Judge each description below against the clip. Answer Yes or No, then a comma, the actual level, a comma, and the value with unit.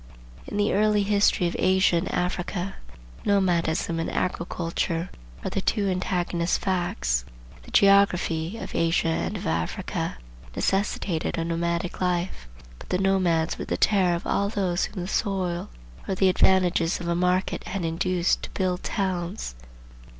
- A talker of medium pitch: Yes, medium, 180 Hz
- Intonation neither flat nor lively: No, narrow, 2.1 semitones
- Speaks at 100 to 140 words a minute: No, average, 150 wpm